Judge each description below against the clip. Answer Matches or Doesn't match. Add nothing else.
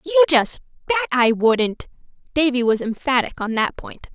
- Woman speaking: Matches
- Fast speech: Doesn't match